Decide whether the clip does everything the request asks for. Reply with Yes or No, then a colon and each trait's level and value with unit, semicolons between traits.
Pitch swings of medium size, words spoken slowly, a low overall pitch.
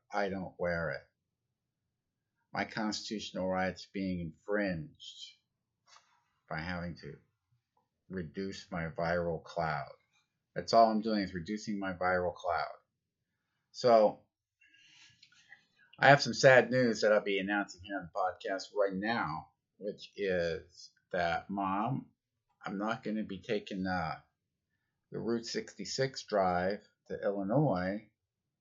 Yes: average, 3.9 semitones; slow, 120 wpm; low, 100 Hz